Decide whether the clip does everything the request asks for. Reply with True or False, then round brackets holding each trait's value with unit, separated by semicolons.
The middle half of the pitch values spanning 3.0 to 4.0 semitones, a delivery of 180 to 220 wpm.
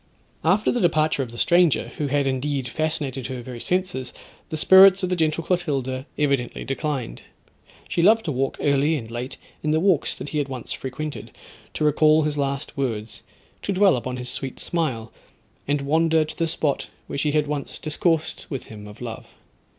True (3.5 semitones; 185 wpm)